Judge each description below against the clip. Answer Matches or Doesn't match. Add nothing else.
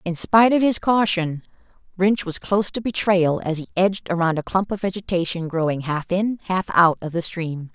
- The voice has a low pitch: Doesn't match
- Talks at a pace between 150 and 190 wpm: Doesn't match